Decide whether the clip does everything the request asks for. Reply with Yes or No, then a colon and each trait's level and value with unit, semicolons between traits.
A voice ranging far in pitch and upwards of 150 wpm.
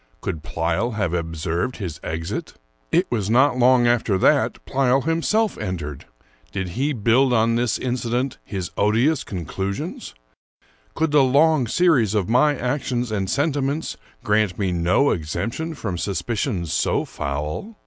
No: wide, 6.5 semitones; average, 140 wpm